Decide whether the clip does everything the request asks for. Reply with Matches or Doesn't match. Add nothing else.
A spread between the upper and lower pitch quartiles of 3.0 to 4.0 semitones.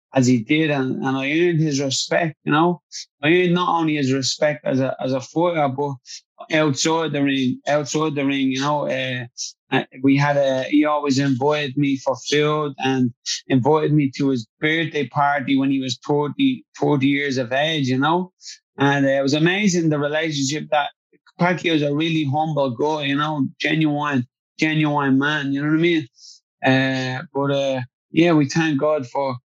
Doesn't match